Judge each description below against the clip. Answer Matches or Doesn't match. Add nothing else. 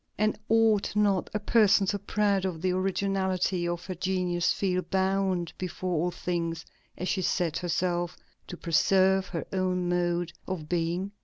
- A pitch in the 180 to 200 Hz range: Matches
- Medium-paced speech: Matches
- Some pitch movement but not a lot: Doesn't match